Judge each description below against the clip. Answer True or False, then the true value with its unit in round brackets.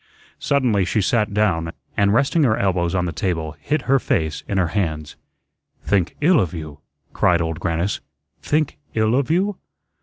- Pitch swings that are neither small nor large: False (7.2 semitones)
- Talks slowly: False (170 wpm)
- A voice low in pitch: True (100 Hz)